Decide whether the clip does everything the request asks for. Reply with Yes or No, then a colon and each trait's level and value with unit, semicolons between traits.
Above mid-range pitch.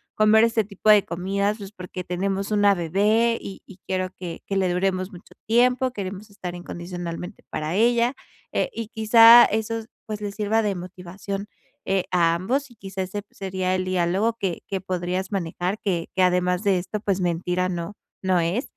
Yes: high, 195 Hz